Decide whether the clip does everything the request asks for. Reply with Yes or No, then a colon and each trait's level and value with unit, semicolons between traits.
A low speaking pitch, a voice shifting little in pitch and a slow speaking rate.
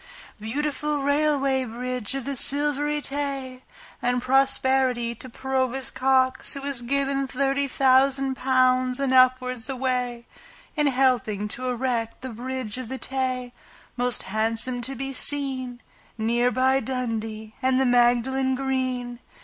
No: very high, 255 Hz; narrow, 1.6 semitones; slow, 130 wpm